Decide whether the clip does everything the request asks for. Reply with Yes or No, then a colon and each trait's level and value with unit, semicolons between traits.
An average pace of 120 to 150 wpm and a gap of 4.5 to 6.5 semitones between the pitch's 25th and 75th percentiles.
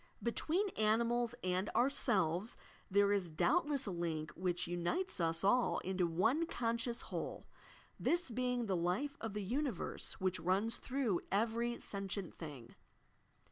Yes: average, 140 wpm; average, 5.2 semitones